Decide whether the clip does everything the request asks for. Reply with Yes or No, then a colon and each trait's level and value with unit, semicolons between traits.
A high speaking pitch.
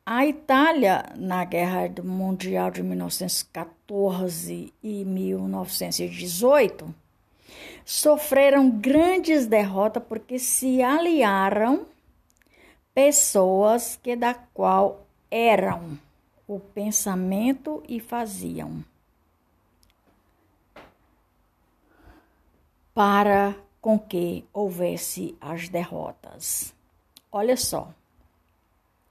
Yes: high, 195 Hz